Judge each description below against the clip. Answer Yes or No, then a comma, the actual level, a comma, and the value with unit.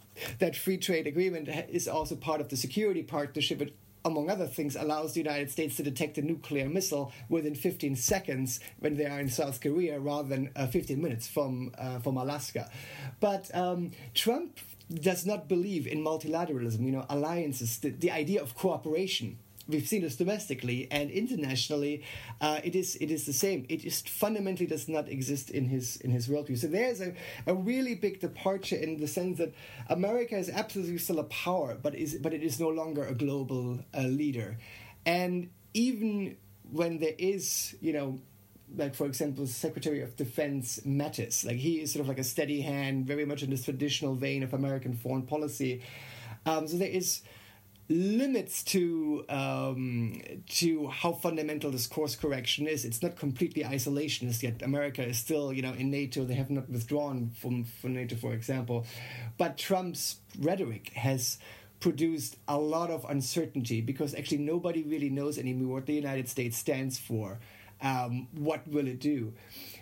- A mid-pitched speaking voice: Yes, medium, 145 Hz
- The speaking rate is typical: Yes, average, 175 wpm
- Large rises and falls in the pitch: No, average, 4.0 semitones